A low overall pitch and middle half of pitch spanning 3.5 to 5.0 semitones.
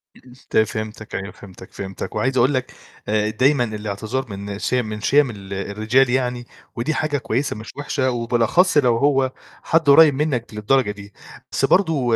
Yes: low, 120 Hz; average, 4.1 semitones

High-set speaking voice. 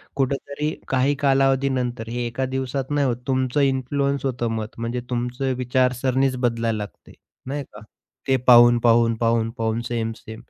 No: low, 125 Hz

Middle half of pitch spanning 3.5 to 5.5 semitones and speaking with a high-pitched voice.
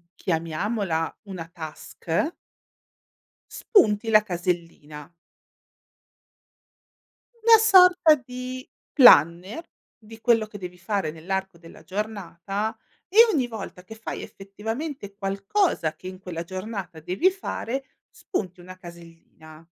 Yes: average, 5.1 semitones; high, 195 Hz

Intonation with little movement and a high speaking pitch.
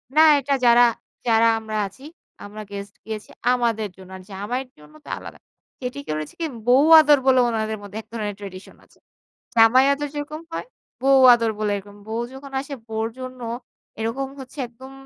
No: average, 4.0 semitones; high, 230 Hz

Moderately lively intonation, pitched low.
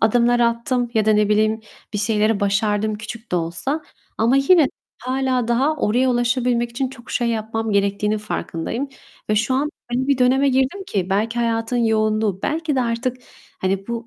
No: average, 3.1 semitones; high, 235 Hz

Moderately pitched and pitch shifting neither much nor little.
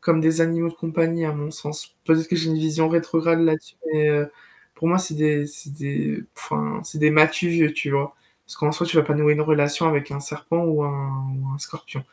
No: medium, 155 Hz; narrow, 2.0 semitones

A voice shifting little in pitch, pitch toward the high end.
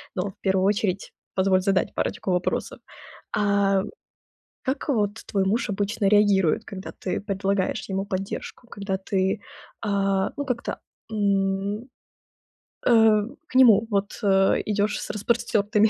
Yes: narrow, 1.6 semitones; high, 200 Hz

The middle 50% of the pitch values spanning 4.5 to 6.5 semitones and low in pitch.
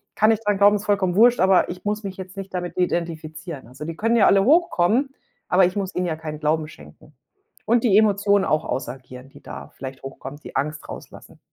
No: average, 4.9 semitones; medium, 185 Hz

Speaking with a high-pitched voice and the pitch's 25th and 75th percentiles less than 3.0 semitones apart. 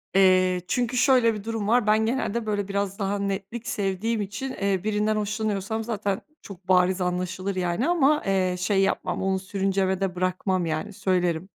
Yes: high, 200 Hz; narrow, 2.6 semitones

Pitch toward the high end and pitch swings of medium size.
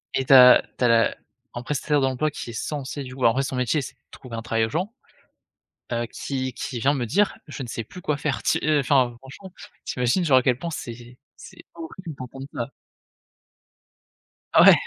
No: low, 130 Hz; average, 3.4 semitones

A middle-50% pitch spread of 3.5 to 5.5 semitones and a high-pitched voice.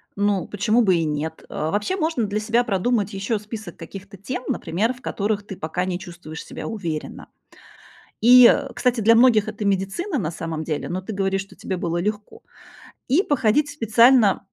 Yes: average, 4.1 semitones; high, 205 Hz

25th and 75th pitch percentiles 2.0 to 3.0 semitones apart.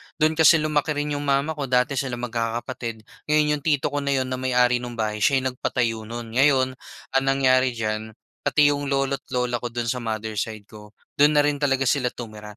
No: average, 3.5 semitones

